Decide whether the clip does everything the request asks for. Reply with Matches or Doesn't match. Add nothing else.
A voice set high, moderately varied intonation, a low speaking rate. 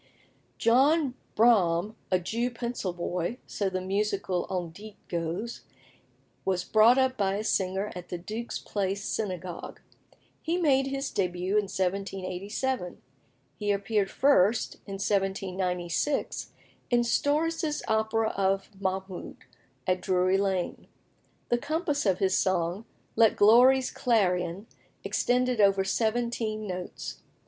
Matches